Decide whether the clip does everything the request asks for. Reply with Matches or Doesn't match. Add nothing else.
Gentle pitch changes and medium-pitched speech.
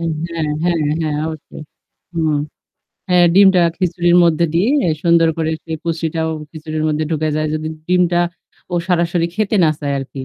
Matches